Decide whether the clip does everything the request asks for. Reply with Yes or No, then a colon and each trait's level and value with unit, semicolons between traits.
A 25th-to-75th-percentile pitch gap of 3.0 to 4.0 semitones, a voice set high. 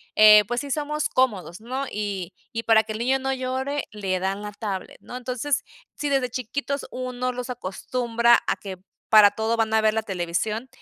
Yes: average, 3.5 semitones; high, 230 Hz